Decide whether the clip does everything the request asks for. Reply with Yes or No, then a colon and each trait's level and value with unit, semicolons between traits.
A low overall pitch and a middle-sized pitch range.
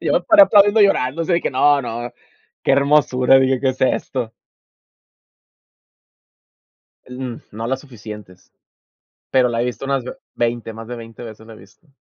Yes: low, 125 Hz; average, 3.1 semitones